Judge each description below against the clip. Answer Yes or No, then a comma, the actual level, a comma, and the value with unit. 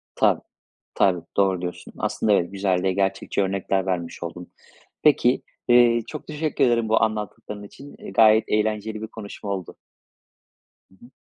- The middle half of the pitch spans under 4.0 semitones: Yes, average, 2.8 semitones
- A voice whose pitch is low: Yes, low, 105 Hz